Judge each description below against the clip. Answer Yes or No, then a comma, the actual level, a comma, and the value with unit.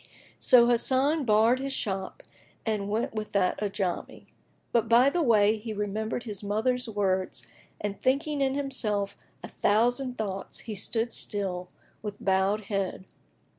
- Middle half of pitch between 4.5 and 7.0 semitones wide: No, average, 3.6 semitones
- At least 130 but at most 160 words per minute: Yes, average, 140 wpm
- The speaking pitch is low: No, high, 215 Hz